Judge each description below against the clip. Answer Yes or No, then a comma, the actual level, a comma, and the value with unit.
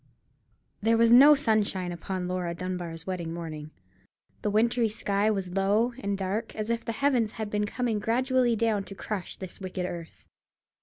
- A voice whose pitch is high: Yes, high, 205 Hz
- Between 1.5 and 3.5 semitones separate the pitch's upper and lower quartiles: No, average, 3.9 semitones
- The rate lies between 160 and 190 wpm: Yes, average, 165 wpm